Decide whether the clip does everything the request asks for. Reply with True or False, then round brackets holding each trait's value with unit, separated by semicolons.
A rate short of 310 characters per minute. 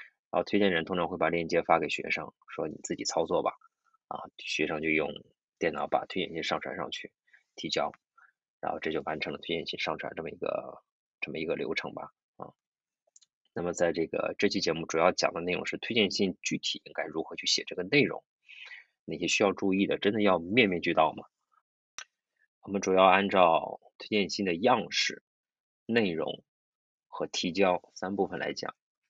True (270 characters per minute)